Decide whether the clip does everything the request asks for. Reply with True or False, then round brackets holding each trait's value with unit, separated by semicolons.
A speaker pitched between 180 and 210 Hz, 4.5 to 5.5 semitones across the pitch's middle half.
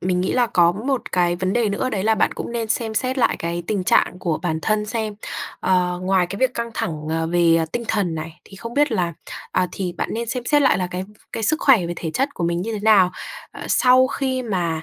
True (200 Hz; 5.1 semitones)